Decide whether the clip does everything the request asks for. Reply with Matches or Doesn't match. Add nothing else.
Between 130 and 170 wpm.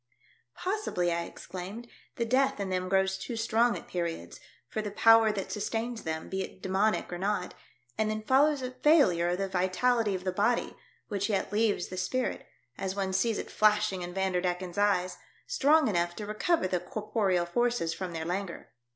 Doesn't match